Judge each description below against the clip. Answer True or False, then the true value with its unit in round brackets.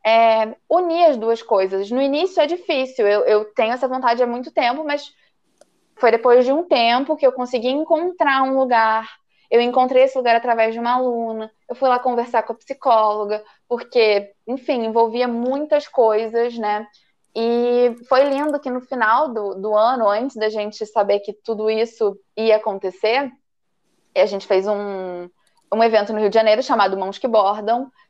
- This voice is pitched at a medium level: False (235 Hz)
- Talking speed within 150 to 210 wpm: True (175 wpm)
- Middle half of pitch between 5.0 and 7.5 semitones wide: False (3.5 semitones)